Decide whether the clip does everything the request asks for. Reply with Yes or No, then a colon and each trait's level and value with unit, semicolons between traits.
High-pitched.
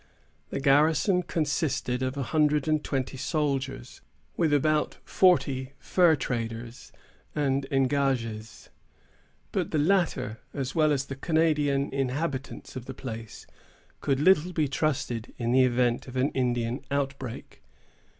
No: low, 135 Hz